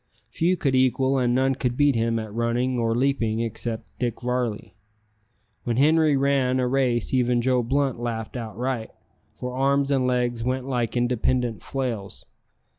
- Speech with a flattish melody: Yes, narrow, 2.2 semitones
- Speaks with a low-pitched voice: Yes, low, 125 Hz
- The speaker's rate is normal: Yes, average, 155 wpm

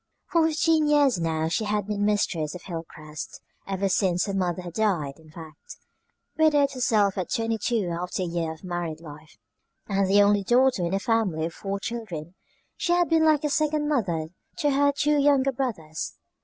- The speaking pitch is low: No, high, 200 Hz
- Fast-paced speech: No, average, 185 wpm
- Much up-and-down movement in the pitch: Yes, wide, 8.1 semitones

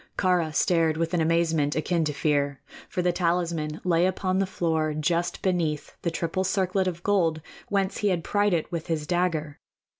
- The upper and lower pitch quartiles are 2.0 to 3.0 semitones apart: Yes, narrow, 2.6 semitones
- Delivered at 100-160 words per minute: No, average, 180 wpm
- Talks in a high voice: No, medium, 170 Hz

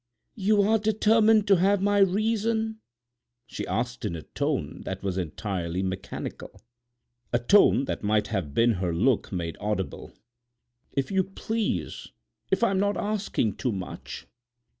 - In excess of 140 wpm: No, slow, 135 wpm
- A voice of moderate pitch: No, low, 125 Hz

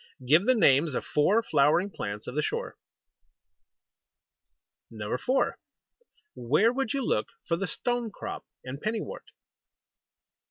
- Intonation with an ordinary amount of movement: No, wide, 8.9 semitones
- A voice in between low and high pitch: Yes, medium, 170 Hz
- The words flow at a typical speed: No, slow, 125 wpm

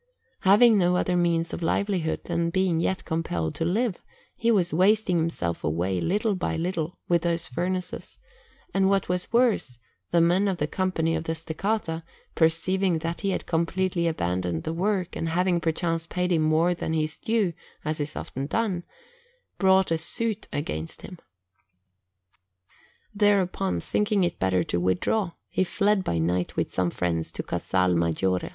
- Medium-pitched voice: Yes, medium, 170 Hz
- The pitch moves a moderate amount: Yes, average, 3.4 semitones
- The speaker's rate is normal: Yes, average, 160 wpm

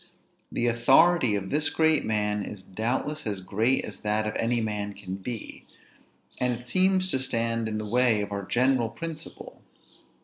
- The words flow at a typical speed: Yes, average, 170 wpm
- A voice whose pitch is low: Yes, low, 115 Hz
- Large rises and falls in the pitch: No, average, 4.0 semitones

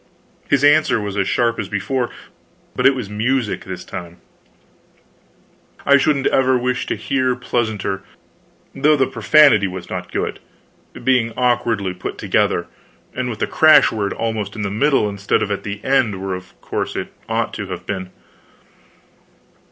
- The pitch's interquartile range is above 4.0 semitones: Yes, average, 4.7 semitones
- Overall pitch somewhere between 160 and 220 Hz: No, low, 115 Hz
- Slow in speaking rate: No, average, 160 wpm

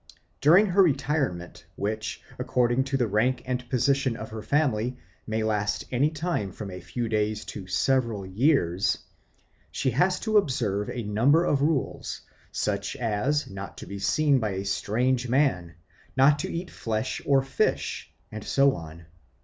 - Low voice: Yes, low, 120 Hz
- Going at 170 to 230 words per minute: No, average, 155 wpm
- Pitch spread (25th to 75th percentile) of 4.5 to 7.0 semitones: Yes, average, 5.1 semitones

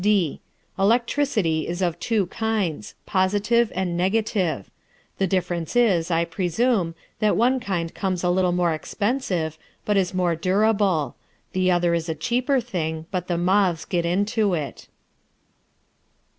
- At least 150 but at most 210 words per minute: No, average, 140 wpm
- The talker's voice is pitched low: No, medium, 185 Hz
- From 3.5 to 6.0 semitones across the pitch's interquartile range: Yes, average, 3.8 semitones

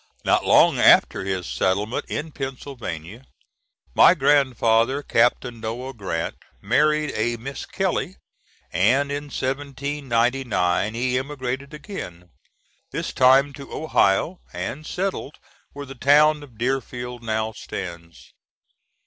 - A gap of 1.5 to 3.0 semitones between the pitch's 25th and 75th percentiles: No, average, 4.4 semitones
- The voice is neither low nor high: No, low, 130 Hz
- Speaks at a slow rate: Yes, slow, 110 wpm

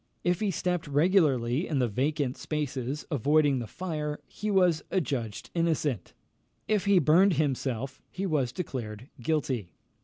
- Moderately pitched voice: Yes, medium, 150 Hz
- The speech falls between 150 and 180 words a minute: No, average, 140 wpm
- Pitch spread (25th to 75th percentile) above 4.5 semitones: Yes, average, 5.1 semitones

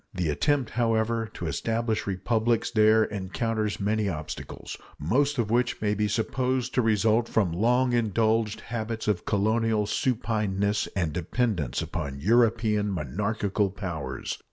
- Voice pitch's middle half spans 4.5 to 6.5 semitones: No, average, 2.7 semitones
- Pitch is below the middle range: Yes, low, 110 Hz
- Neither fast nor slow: No, slow, 130 wpm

